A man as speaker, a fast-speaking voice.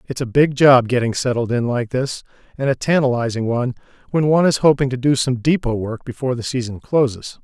Yes: male; fast, 210 wpm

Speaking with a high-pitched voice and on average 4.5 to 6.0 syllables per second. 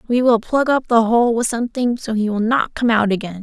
Yes: high, 230 Hz; 5.5 syllables/s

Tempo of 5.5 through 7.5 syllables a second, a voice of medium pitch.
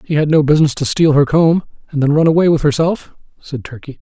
Yes: 6.2 syllables/s; medium, 150 Hz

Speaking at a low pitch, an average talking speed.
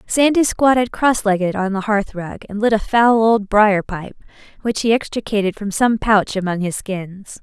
No: high, 210 Hz; average, 185 wpm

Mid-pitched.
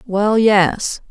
No: high, 205 Hz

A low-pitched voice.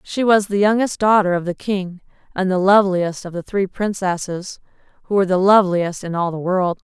No: high, 190 Hz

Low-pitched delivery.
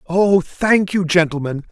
No: medium, 175 Hz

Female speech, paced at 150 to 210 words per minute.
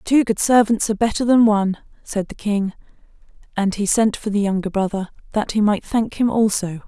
Yes: female; average, 200 wpm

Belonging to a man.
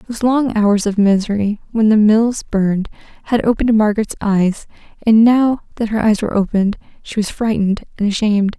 No: female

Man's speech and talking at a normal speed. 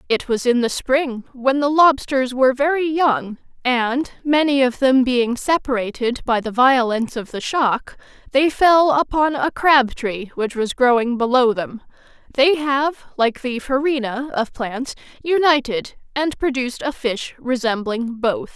No: female; average, 155 wpm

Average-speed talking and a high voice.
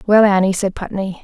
Yes: average, 195 wpm; high, 195 Hz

